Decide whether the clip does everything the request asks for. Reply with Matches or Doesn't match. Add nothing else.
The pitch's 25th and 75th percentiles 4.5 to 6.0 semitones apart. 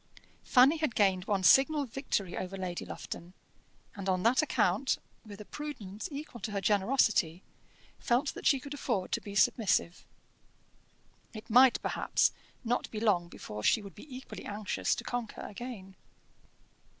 Matches